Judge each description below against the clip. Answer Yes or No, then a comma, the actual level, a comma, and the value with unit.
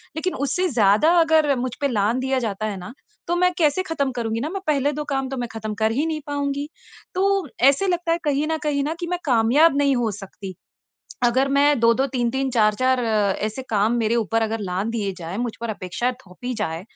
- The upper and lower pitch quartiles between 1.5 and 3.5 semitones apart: No, average, 5.0 semitones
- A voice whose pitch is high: Yes, very high, 255 Hz